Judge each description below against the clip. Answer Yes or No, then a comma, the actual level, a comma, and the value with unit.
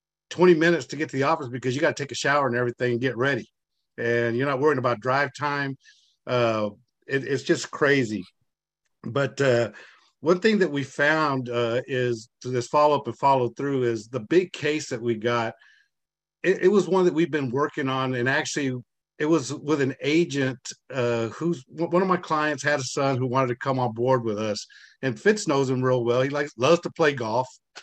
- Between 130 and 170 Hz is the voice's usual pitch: Yes, low, 135 Hz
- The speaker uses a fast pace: Yes, fast, 210 wpm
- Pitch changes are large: No, average, 3.8 semitones